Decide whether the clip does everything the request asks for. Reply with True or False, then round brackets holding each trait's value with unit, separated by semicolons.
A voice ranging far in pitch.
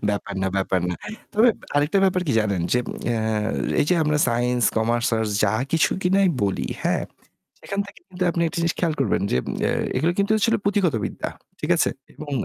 True (8.4 semitones)